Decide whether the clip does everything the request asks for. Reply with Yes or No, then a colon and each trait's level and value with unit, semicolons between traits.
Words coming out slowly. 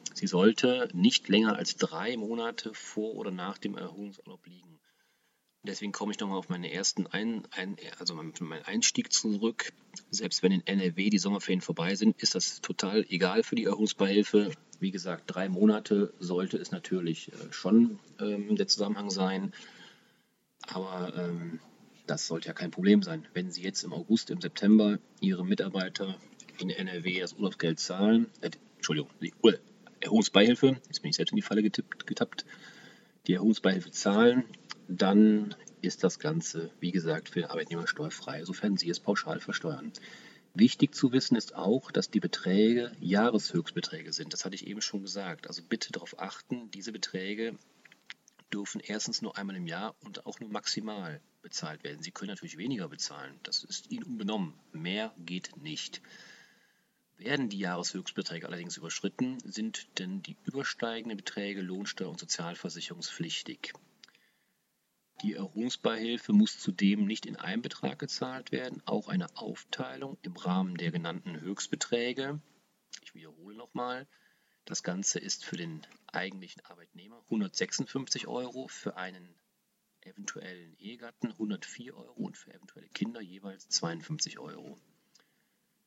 No: average, 145 wpm